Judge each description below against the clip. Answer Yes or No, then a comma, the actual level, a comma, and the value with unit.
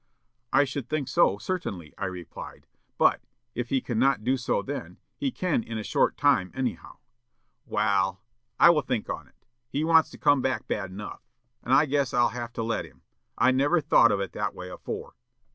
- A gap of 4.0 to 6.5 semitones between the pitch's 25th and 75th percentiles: Yes, wide, 5.5 semitones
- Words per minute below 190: No, average, 195 wpm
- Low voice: Yes, low, 125 Hz